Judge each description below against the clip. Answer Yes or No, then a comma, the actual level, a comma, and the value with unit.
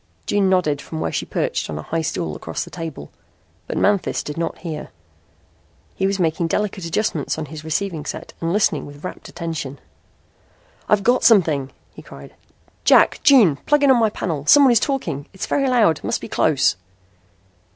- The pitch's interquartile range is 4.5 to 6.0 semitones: Yes, wide, 5.5 semitones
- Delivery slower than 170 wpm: No, average, 180 wpm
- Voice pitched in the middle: Yes, medium, 170 Hz